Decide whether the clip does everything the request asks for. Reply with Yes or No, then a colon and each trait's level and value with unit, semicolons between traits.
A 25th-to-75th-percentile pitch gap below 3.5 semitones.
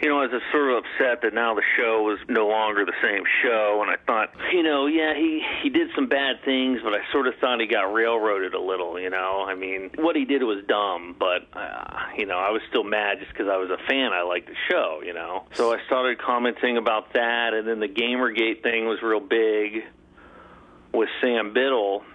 No: average, 4.0 semitones